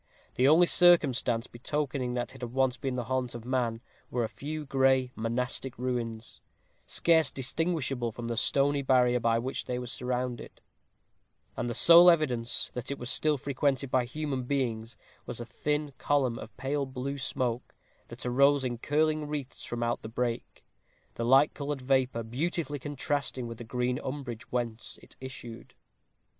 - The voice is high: No, low, 130 Hz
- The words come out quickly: No, average, 165 wpm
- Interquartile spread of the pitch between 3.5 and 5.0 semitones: No, average, 2.8 semitones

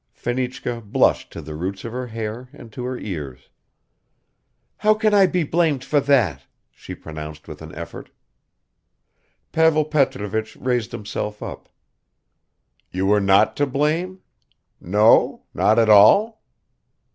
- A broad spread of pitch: Yes, wide, 6.2 semitones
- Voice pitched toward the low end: Yes, low, 120 Hz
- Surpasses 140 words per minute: No, slow, 135 wpm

